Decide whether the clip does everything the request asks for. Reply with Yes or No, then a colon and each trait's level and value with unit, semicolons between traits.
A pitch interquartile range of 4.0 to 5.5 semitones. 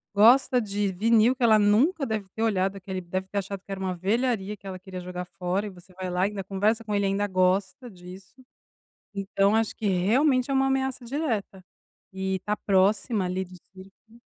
No: average, 3.2 semitones